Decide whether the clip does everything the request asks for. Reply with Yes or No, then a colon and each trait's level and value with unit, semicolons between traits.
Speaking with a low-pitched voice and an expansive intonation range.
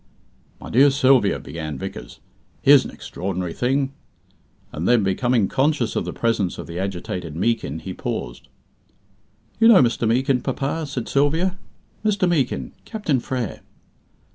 Yes: low, 125 Hz; wide, 6.8 semitones